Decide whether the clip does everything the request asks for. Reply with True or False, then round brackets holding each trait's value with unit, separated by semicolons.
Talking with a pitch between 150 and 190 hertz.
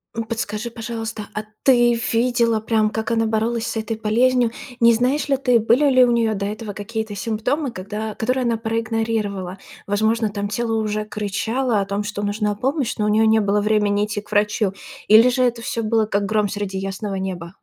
False (220 Hz)